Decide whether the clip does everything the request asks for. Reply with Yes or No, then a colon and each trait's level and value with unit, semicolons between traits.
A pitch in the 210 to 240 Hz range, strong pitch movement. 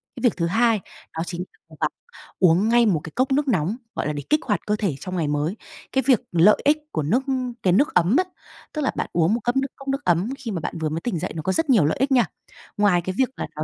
No: high, 200 Hz; wide, 7.0 semitones